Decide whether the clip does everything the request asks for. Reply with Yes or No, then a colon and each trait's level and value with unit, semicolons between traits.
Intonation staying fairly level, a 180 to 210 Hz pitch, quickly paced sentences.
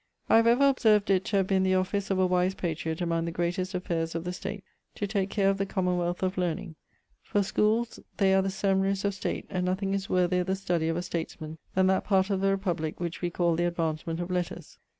Yes: narrow, 2.1 semitones; medium, 185 Hz; fast, 235 wpm